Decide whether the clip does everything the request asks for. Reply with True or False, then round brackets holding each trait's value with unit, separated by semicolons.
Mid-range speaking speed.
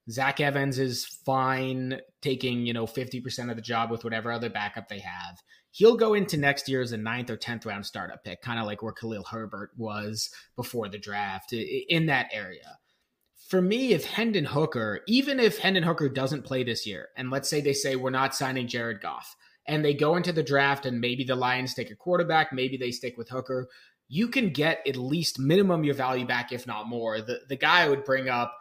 False (220 wpm)